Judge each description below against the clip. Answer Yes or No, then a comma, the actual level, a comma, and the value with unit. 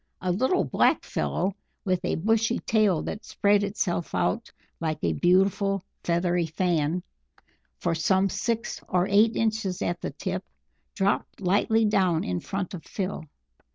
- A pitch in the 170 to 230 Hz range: Yes, high, 190 Hz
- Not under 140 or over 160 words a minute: Yes, average, 145 wpm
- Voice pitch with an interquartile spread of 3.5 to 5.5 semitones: No, average, 3.0 semitones